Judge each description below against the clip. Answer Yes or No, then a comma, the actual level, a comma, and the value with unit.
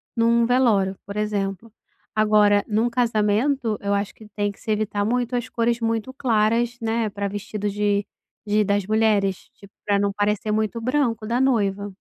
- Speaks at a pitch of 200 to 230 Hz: Yes, high, 215 Hz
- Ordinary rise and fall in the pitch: No, narrow, 2.2 semitones